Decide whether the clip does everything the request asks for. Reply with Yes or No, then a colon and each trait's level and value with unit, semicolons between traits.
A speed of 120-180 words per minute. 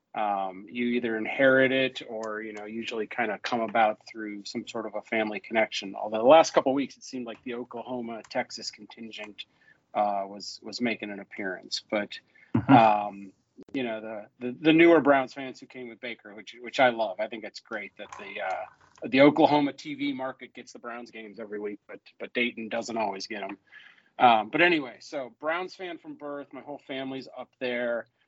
No: average, 200 wpm